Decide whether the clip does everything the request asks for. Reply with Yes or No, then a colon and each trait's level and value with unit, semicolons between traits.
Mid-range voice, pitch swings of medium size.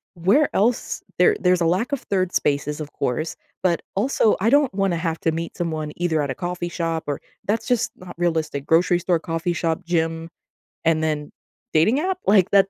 Yes: medium, 175 Hz; average, 3.3 semitones